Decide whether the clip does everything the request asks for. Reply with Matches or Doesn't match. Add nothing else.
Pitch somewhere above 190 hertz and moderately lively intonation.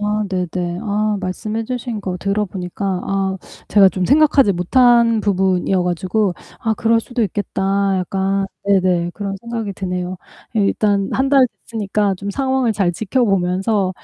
Matches